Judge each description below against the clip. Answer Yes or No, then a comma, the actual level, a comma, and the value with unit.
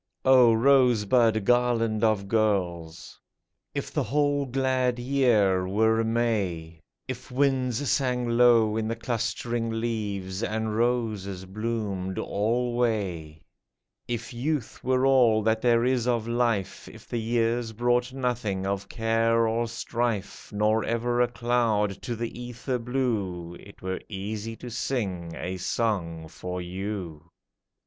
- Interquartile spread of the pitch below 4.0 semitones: Yes, average, 3.4 semitones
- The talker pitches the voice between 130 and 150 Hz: No, low, 115 Hz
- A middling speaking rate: No, slow, 125 wpm